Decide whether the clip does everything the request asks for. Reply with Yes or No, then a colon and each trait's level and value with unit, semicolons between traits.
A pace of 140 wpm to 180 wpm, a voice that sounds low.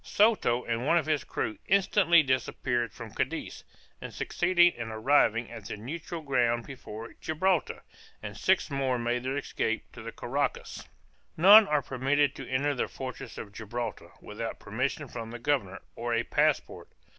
Yes: average, 160 wpm; low, 130 Hz